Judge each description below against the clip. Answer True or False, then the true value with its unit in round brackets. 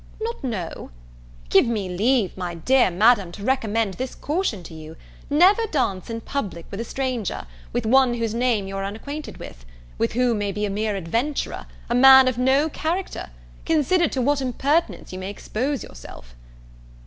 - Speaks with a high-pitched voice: True (235 Hz)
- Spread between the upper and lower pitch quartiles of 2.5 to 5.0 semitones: False (5.5 semitones)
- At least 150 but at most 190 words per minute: True (170 wpm)